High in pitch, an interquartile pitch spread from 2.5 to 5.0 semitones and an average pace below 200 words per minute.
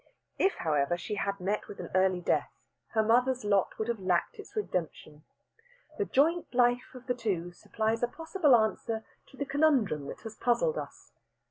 No: high, 225 Hz; wide, 5.6 semitones; average, 175 wpm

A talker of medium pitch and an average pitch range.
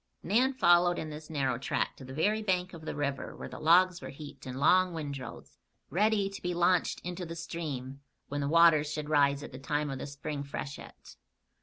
Yes: medium, 155 Hz; average, 3.9 semitones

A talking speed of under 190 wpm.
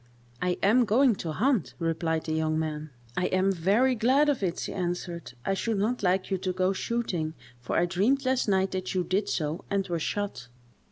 No: fast, 205 wpm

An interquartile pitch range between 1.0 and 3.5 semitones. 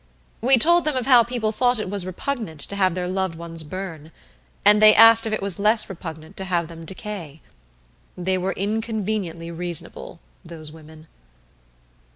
No: average, 4.6 semitones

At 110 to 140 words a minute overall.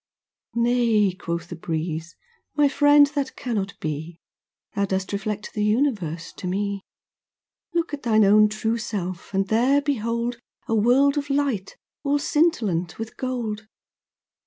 Yes: slow, 135 wpm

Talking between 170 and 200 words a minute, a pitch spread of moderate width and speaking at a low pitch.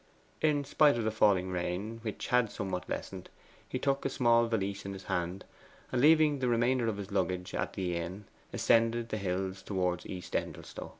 Yes: average, 185 wpm; average, 4.2 semitones; low, 105 Hz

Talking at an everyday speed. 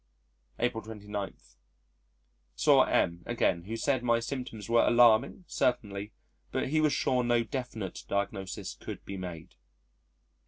No: slow, 125 wpm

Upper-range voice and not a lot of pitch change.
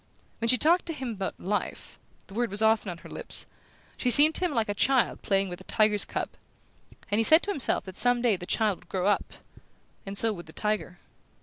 No: high, 215 Hz; average, 4.0 semitones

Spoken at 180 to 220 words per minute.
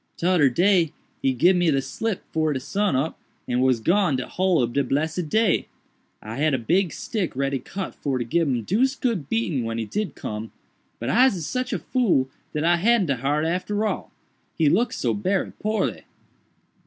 Yes: average, 185 wpm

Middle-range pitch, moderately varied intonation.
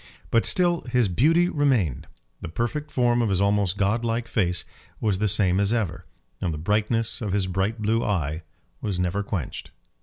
No: low, 105 Hz; average, 3.9 semitones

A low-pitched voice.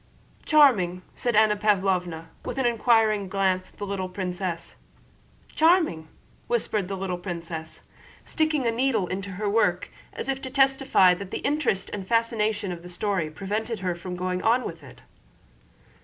No: high, 200 Hz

